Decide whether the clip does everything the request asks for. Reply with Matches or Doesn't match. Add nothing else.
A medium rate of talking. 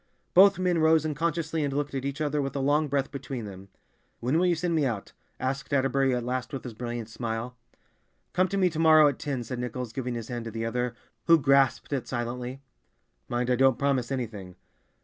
Doesn't match